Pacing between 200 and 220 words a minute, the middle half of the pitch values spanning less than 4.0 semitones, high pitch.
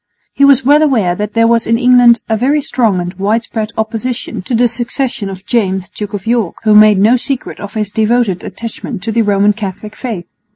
Yes: fast, 205 wpm; average, 3.0 semitones; high, 220 Hz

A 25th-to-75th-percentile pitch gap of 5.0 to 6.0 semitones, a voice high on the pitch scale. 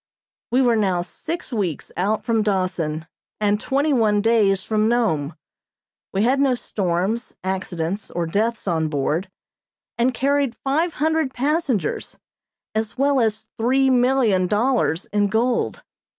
Yes: average, 5.3 semitones; high, 220 Hz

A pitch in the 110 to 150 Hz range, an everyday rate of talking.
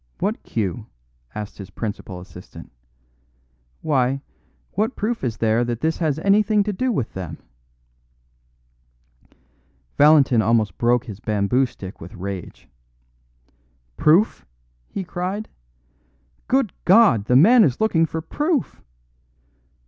No: low, 135 Hz; slow, 115 wpm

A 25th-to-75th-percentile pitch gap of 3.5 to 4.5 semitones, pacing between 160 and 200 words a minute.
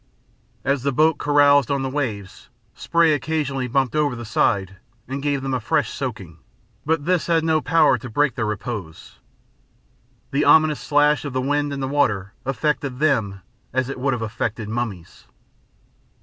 Yes: average, 3.8 semitones; average, 165 wpm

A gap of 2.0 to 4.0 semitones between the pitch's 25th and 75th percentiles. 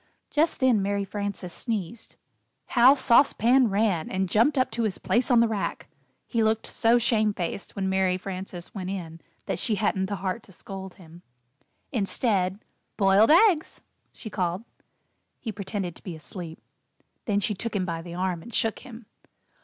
Yes: average, 3.7 semitones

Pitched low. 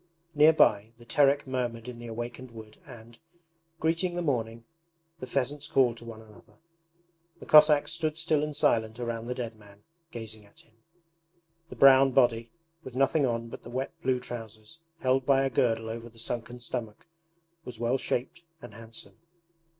Yes: low, 120 Hz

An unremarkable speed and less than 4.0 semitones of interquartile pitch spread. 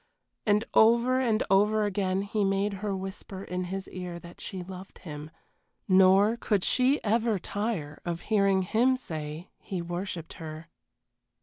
Yes: average, 145 wpm; average, 3.0 semitones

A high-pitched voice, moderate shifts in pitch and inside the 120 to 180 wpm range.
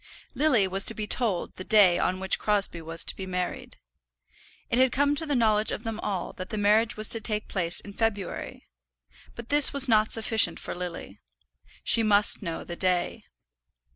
No: high, 210 Hz; average, 3.5 semitones; average, 190 wpm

